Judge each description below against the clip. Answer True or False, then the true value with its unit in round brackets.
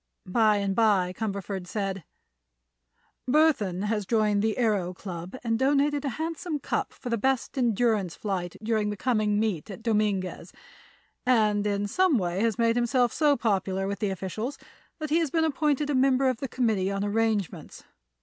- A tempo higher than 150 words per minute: True (170 wpm)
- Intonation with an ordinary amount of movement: True (4.4 semitones)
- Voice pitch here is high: True (220 Hz)